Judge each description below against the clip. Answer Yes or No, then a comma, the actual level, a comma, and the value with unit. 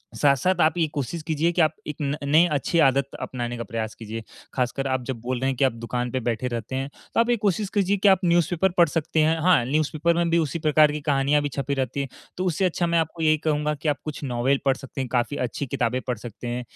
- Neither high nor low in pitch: Yes, medium, 145 Hz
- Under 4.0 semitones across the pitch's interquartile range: No, average, 4.3 semitones